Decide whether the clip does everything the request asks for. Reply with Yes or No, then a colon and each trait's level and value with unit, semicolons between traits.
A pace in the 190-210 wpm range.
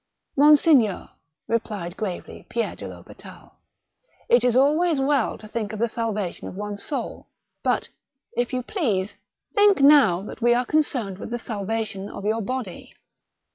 No: average, 160 wpm